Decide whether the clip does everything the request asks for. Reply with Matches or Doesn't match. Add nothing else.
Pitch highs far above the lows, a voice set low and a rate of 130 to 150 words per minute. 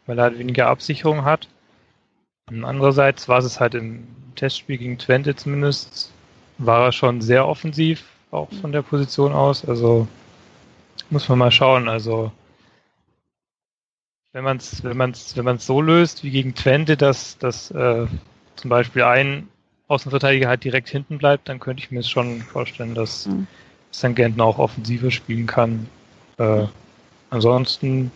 Doesn't match